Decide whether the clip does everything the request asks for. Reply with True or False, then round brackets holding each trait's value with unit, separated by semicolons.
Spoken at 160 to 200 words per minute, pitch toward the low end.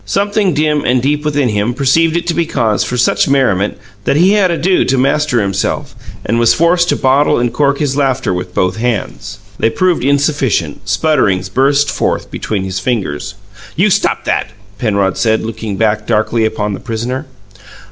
True (180 wpm; 125 Hz)